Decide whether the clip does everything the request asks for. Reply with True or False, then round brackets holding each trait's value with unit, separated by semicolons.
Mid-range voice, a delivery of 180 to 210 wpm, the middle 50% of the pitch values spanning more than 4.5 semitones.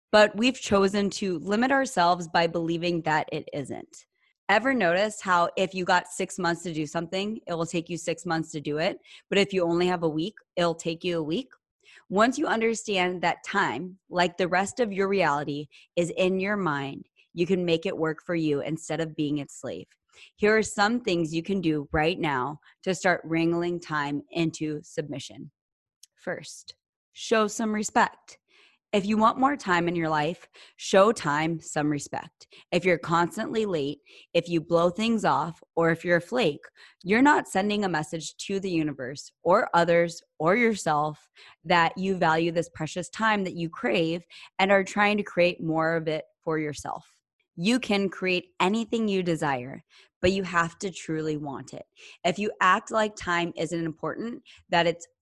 False (175 Hz; 185 wpm; 3.4 semitones)